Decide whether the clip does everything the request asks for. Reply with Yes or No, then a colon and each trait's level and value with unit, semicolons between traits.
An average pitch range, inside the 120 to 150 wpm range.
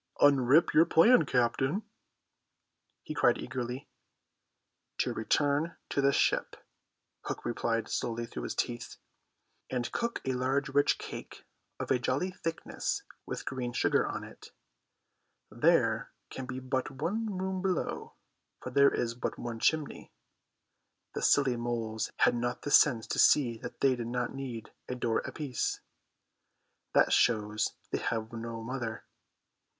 Yes: average, 3.4 semitones; average, 140 wpm